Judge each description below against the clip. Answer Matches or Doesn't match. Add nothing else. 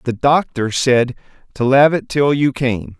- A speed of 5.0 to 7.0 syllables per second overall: Doesn't match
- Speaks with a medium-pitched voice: Doesn't match